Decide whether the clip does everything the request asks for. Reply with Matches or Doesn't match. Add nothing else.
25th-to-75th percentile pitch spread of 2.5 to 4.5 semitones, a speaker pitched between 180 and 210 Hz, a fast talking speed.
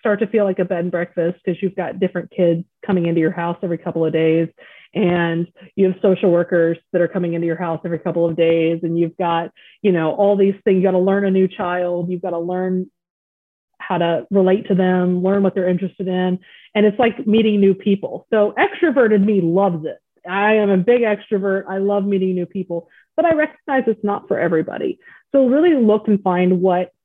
Matches